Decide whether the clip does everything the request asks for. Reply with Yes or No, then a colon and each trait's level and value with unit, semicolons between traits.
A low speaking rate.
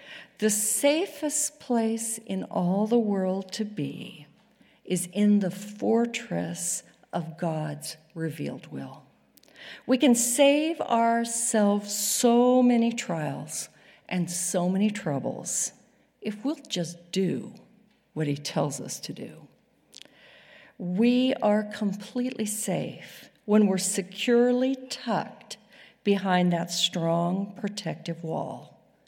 Yes: slow, 105 wpm